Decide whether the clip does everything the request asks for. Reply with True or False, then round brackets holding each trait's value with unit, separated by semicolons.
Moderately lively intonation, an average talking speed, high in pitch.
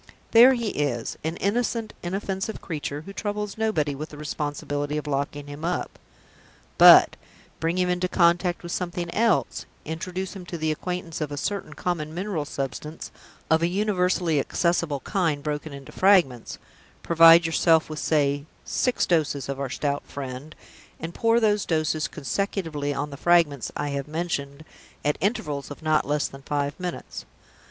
False (3.9 semitones; 160 wpm; 160 Hz)